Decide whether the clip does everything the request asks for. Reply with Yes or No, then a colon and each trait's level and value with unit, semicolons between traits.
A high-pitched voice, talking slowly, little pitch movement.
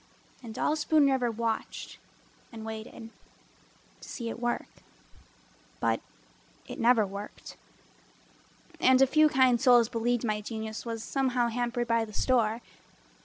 Yes: high, 235 Hz; slow, 130 wpm; narrow, 2.1 semitones